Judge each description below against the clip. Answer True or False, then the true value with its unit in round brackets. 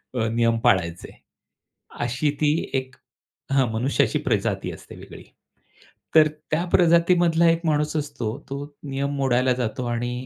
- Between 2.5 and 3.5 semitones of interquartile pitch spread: False (4.2 semitones)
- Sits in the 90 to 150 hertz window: True (135 Hz)